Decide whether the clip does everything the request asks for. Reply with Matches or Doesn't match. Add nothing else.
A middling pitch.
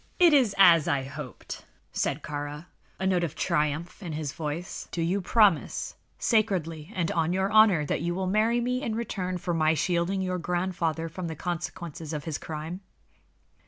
Matches